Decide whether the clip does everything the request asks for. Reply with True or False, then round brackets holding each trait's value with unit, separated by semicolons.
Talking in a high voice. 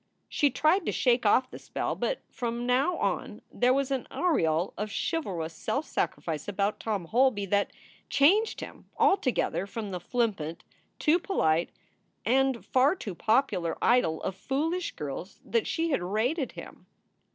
True (240 Hz)